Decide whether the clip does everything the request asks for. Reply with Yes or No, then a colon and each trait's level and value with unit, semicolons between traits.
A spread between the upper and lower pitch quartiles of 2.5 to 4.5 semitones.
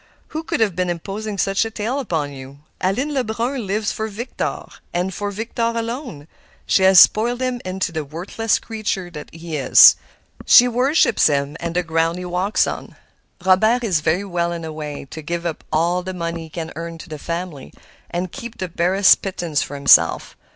No: average, 4.9 semitones